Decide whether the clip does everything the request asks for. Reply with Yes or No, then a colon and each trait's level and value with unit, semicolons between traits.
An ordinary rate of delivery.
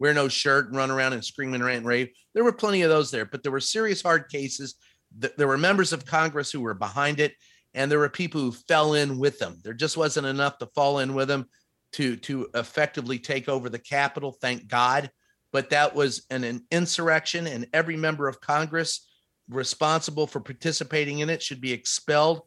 No: fast, 210 wpm